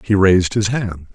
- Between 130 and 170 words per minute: No, fast, 210 wpm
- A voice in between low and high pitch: No, low, 100 Hz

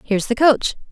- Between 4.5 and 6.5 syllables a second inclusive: No, 8.0 syllables/s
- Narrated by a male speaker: No, female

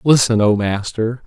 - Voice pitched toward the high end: No, low, 115 Hz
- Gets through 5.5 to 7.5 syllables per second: No, 4.3 syllables/s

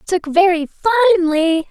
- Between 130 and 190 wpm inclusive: Yes, average, 140 wpm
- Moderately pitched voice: No, very high, 360 Hz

